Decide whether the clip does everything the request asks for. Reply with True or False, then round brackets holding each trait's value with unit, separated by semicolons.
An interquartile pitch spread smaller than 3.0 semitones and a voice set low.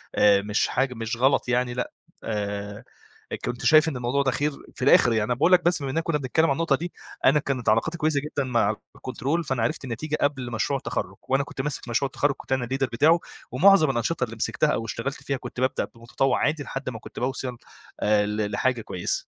False (3.7 semitones; 130 Hz)